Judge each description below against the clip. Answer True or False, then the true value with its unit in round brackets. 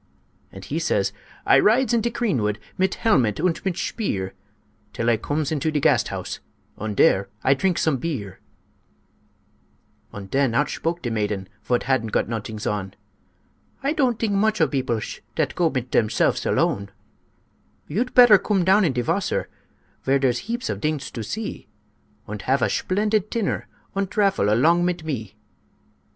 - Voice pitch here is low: False (150 Hz)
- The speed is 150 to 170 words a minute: True (160 wpm)